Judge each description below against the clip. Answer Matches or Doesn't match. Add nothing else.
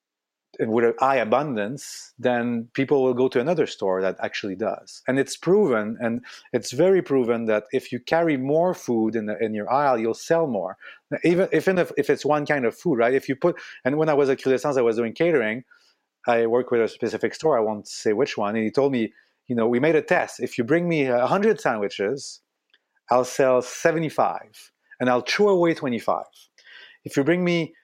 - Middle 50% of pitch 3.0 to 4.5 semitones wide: Doesn't match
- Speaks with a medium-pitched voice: Doesn't match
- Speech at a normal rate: Doesn't match